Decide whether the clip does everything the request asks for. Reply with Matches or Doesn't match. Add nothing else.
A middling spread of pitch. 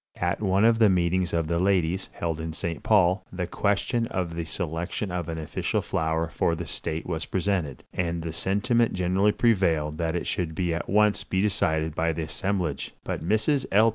Matches